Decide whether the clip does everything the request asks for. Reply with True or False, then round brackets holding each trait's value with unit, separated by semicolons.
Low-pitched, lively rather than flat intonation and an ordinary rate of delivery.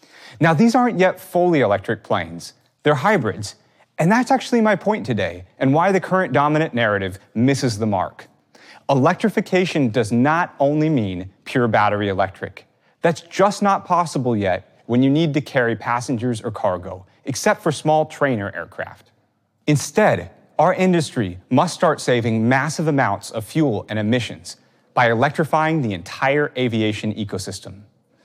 False (130 Hz; 7.4 semitones; 145 wpm)